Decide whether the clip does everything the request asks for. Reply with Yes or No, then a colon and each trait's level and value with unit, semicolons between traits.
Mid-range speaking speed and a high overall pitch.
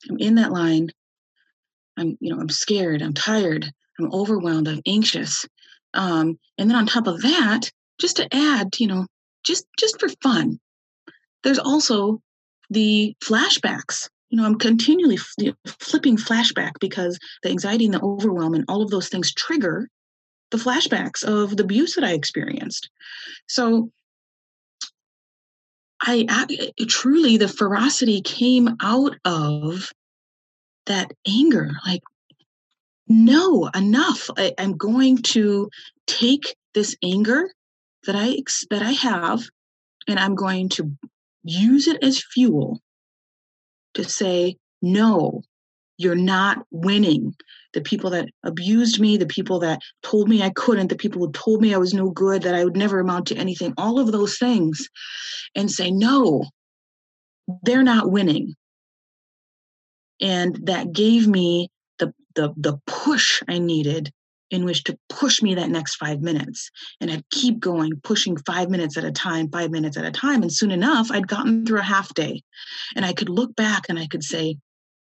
Yes: average, 150 wpm; high, 205 Hz